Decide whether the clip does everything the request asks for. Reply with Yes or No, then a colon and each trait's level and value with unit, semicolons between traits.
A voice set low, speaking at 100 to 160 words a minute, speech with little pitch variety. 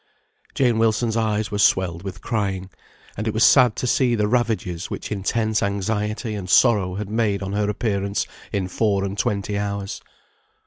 No: low, 105 Hz; average, 170 wpm; narrow, 2.1 semitones